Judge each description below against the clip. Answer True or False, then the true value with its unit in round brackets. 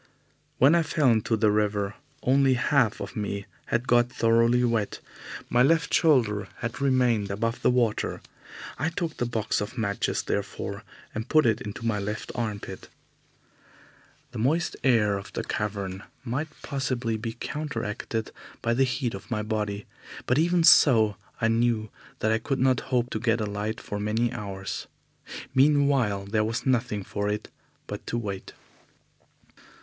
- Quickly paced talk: False (155 wpm)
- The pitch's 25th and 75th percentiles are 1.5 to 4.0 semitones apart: True (3.5 semitones)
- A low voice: True (115 Hz)